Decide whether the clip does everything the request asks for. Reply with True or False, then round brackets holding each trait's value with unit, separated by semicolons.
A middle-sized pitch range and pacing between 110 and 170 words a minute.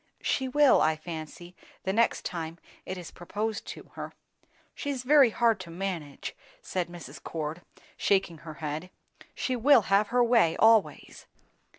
False (5.9 semitones; 155 wpm)